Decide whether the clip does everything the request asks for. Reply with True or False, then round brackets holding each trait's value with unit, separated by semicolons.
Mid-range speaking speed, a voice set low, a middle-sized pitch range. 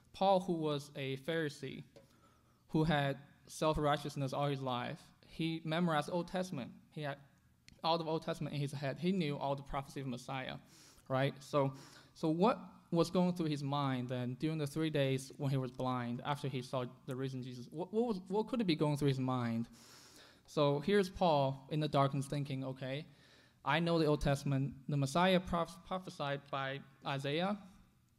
False (185 wpm; 145 Hz; 3.3 semitones)